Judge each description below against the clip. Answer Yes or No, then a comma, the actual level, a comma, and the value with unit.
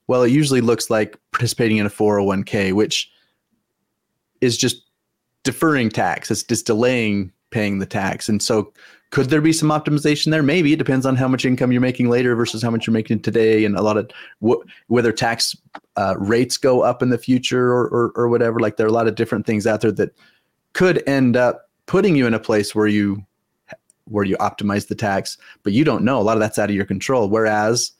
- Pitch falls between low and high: No, low, 115 Hz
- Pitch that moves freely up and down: No, average, 2.9 semitones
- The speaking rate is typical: No, fast, 215 wpm